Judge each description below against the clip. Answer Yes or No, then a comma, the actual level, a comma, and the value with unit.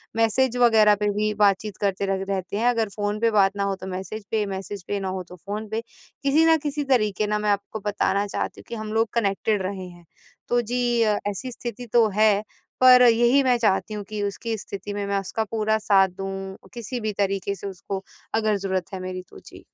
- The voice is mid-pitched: No, high, 210 Hz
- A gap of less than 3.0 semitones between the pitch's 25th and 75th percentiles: Yes, narrow, 2.5 semitones